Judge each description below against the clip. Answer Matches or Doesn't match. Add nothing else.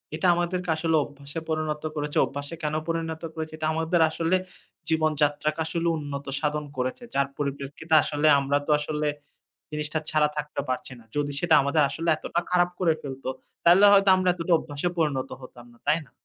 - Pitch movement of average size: Doesn't match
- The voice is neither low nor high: Matches